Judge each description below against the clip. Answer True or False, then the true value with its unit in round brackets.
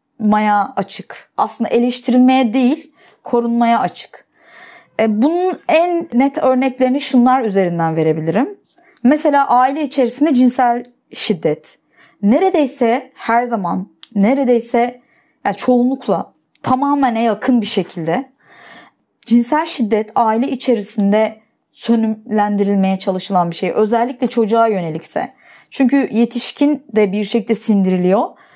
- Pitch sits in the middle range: False (235 Hz)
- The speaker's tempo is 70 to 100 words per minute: True (95 wpm)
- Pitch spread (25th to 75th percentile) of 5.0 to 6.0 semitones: False (3.8 semitones)